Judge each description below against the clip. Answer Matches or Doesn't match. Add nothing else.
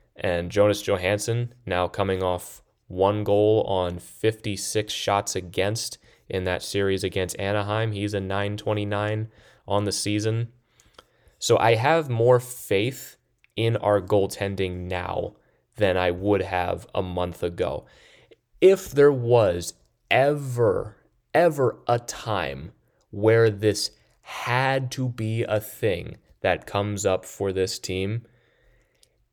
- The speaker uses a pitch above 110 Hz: Doesn't match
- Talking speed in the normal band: Doesn't match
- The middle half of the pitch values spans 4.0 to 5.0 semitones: Doesn't match